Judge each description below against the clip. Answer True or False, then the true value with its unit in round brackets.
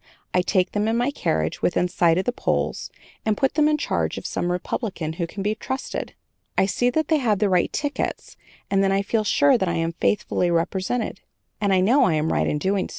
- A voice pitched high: True (195 Hz)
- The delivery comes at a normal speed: False (230 wpm)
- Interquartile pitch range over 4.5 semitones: True (5.5 semitones)